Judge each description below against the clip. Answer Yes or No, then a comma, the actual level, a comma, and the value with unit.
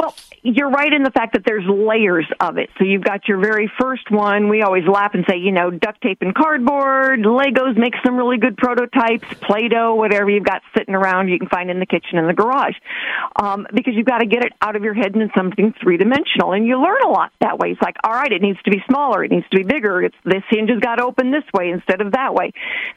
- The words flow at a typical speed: No, fast, 260 wpm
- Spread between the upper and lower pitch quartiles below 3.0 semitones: No, average, 4.3 semitones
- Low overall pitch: No, high, 220 Hz